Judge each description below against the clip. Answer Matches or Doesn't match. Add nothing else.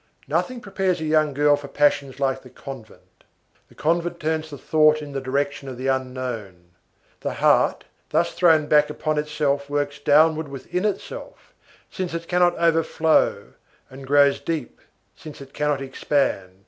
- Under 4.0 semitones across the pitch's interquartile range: Matches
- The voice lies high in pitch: Doesn't match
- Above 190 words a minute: Doesn't match